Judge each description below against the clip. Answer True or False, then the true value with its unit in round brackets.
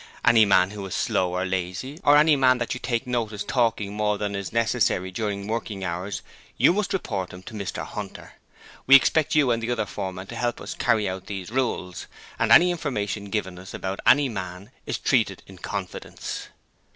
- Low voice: True (105 Hz)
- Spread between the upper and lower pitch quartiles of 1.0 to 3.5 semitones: False (4.4 semitones)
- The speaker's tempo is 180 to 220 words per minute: True (195 wpm)